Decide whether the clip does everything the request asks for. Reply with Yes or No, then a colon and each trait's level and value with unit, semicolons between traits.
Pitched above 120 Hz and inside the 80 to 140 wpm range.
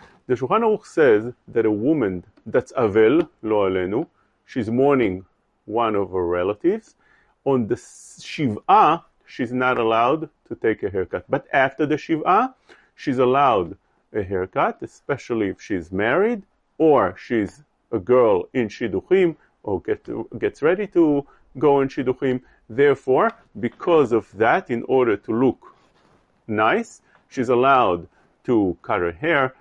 Yes: medium, 140 Hz; slow, 135 wpm